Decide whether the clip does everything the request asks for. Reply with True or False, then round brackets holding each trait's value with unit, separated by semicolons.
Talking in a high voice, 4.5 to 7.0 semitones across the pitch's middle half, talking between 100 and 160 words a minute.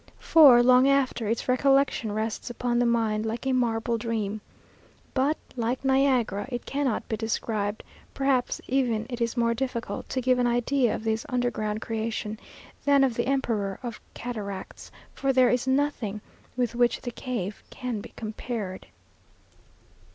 False (240 Hz; 2.7 semitones; 150 wpm)